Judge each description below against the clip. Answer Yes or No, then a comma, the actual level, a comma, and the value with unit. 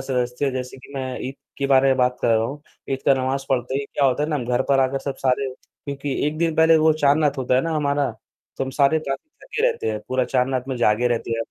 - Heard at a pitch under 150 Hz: Yes, low, 135 Hz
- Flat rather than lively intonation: Yes, narrow, 2.1 semitones